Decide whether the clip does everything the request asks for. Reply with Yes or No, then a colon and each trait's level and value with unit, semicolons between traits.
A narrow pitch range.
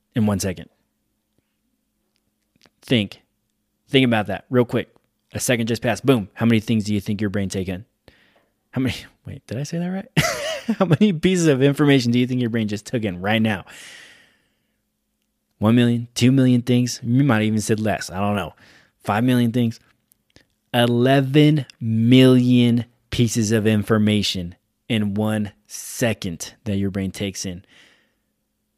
No: average, 3.2 semitones